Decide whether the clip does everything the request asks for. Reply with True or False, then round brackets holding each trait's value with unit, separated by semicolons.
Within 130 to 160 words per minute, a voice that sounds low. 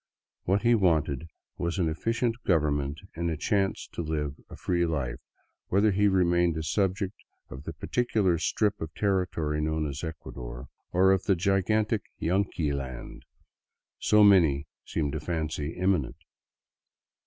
True (150 wpm; 85 Hz)